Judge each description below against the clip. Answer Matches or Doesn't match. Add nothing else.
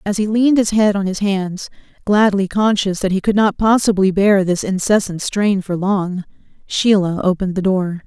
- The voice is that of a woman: Matches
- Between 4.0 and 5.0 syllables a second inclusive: Matches